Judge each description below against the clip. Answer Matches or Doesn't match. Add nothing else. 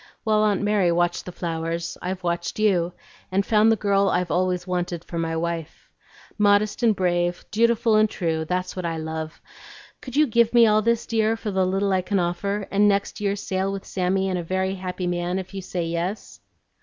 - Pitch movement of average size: Matches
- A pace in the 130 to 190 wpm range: Doesn't match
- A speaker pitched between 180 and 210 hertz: Matches